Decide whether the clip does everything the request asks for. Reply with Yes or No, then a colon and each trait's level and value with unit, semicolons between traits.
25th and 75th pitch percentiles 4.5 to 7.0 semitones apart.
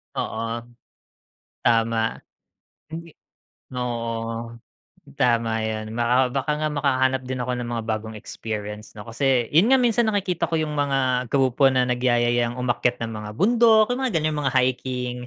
No: average, 3.9 semitones